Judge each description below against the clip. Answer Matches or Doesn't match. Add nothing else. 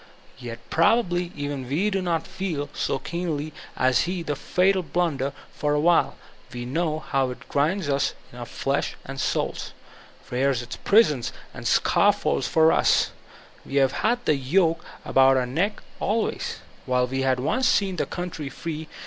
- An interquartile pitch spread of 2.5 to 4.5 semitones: Doesn't match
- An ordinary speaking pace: Matches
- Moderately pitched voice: Matches